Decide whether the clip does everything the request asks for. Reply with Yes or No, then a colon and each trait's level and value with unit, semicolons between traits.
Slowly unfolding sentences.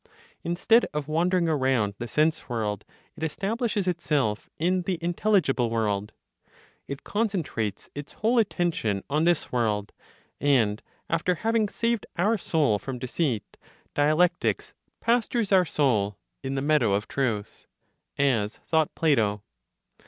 Yes: slow, 125 wpm